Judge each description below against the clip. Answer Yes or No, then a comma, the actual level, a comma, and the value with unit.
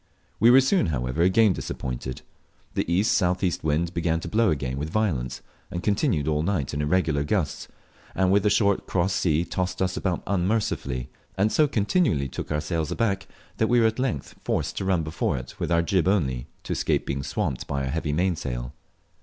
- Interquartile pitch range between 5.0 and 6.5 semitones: Yes, wide, 5.5 semitones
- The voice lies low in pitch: Yes, very low, 85 Hz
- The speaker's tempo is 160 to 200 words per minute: Yes, average, 190 wpm